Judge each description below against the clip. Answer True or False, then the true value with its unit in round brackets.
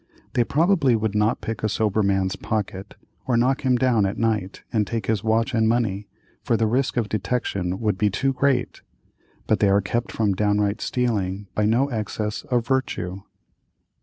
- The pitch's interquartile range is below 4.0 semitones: True (3.0 semitones)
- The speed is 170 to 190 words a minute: True (180 wpm)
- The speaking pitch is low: True (110 Hz)